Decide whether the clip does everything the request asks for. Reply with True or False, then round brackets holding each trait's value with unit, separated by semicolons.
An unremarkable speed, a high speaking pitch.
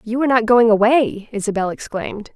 True (155 wpm; 225 Hz)